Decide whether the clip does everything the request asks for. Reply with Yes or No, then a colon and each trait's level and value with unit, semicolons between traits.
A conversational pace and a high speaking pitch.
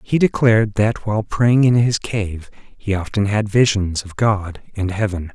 No: average, 180 wpm; low, 105 Hz